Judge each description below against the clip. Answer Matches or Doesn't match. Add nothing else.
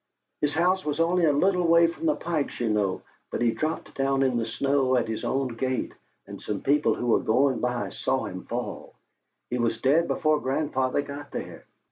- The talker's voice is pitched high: Doesn't match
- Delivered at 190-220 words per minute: Matches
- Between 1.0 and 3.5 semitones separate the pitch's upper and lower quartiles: Doesn't match